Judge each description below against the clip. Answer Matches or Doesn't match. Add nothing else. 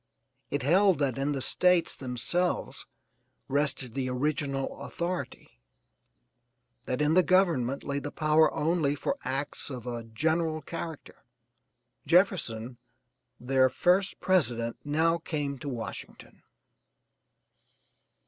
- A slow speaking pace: Matches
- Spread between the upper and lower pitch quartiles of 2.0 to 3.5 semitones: Doesn't match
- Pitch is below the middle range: Doesn't match